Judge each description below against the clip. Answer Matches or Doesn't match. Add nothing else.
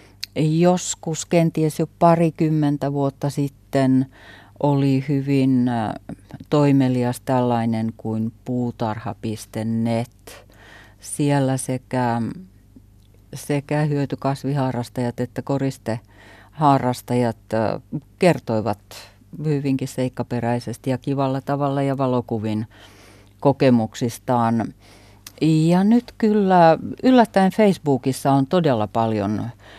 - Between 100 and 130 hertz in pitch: Matches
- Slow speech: Matches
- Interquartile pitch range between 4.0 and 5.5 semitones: Matches